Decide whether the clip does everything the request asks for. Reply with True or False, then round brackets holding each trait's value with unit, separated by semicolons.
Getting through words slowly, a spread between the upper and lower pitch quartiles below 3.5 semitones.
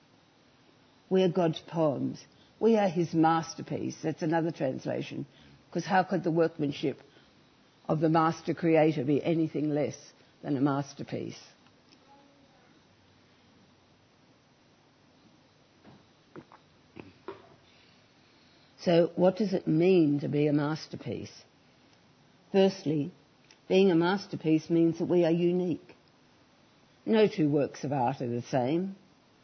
True (105 wpm; 2.8 semitones)